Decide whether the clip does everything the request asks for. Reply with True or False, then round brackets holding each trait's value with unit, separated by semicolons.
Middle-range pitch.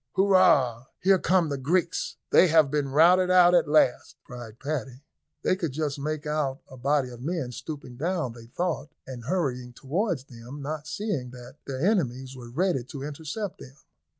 True (145 Hz)